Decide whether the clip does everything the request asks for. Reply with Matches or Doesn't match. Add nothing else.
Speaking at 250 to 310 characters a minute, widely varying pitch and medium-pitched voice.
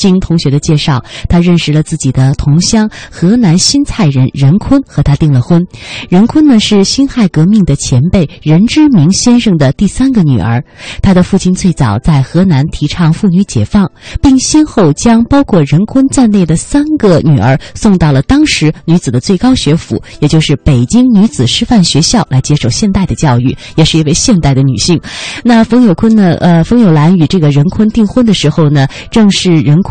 Matches